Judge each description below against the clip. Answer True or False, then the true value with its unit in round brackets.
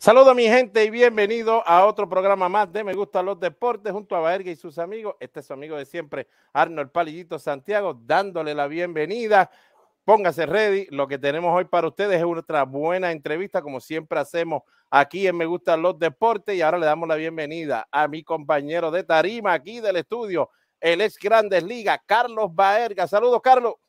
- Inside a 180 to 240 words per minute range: True (190 wpm)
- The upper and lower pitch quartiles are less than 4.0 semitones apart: False (4.5 semitones)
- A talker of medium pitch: True (175 Hz)